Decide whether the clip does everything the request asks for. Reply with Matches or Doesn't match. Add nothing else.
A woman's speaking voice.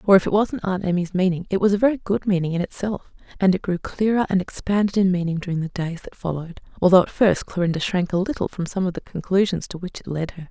Matches